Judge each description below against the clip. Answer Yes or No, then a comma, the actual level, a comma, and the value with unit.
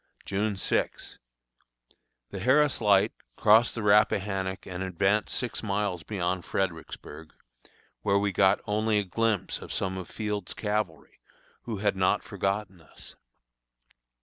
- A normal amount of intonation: No, narrow, 2.1 semitones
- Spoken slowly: Yes, slow, 125 wpm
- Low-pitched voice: Yes, low, 100 Hz